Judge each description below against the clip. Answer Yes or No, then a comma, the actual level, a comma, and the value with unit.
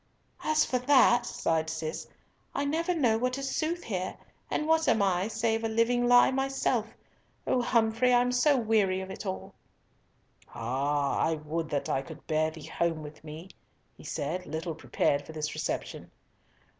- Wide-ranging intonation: Yes, wide, 7.8 semitones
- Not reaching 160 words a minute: No, average, 170 wpm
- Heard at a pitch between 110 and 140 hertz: No, high, 220 Hz